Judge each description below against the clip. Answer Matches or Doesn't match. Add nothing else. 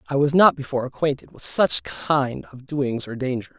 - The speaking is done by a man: Matches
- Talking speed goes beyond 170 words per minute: Matches